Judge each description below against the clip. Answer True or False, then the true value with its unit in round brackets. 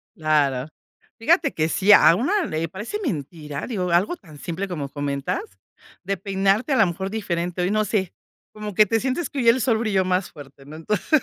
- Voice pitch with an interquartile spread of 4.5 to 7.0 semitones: True (5.5 semitones)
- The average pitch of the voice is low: False (190 Hz)